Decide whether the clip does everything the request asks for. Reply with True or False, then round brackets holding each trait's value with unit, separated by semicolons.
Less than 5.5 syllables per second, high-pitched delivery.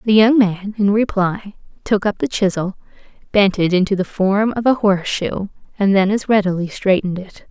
True (5.1 syllables/s; 200 Hz)